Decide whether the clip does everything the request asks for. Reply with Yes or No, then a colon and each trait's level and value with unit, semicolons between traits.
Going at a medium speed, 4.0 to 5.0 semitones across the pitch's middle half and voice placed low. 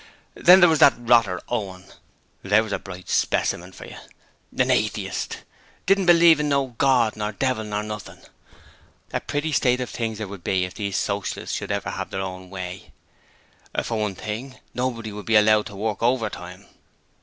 Yes: average, 180 wpm; average, 4.4 semitones; low, 110 Hz